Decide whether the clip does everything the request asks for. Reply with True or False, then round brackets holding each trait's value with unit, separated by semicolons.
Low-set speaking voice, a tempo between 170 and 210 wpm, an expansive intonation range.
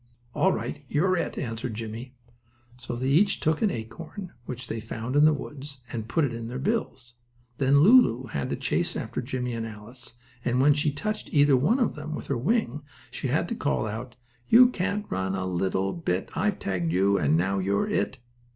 True (130 Hz; 200 wpm; 5.7 semitones)